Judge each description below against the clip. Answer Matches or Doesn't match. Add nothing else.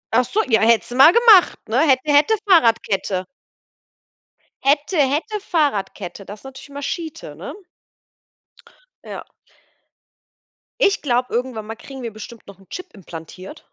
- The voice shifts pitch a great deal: Matches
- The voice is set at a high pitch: Matches